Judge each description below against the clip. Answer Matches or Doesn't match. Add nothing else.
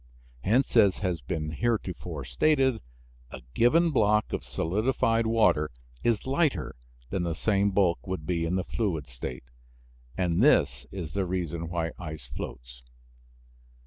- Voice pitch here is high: Doesn't match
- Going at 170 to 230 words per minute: Doesn't match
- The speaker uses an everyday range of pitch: Doesn't match